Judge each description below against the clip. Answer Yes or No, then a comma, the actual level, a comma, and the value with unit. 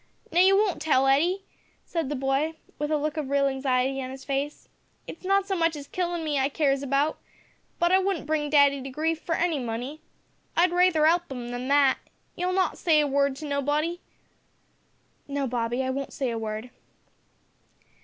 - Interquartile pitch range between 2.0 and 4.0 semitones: Yes, average, 3.5 semitones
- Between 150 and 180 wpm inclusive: No, average, 190 wpm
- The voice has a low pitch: No, very high, 290 Hz